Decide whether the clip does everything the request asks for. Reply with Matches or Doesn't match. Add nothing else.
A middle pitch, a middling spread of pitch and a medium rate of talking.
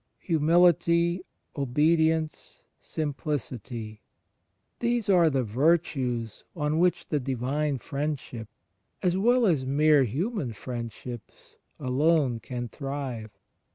Doesn't match